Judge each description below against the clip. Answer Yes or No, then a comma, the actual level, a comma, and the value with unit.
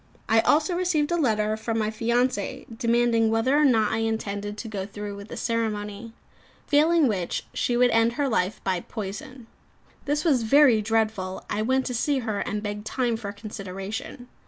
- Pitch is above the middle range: Yes, high, 225 Hz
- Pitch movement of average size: Yes, average, 3.4 semitones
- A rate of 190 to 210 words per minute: No, average, 175 wpm